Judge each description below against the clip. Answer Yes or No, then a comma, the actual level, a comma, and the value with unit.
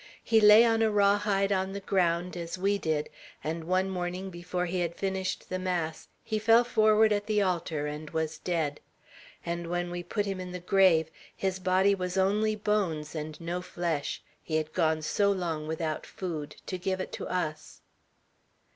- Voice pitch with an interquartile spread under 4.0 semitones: Yes, average, 3.1 semitones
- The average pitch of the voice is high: No, medium, 180 Hz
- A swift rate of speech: No, average, 185 wpm